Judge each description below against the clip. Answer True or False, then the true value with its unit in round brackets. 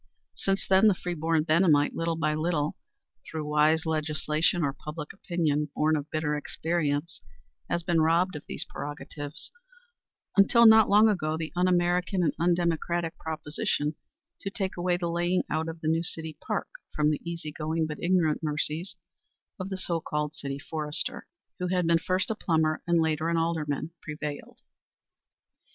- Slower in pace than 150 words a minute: False (165 wpm)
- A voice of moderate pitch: True (160 Hz)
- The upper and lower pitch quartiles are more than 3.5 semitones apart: False (2.4 semitones)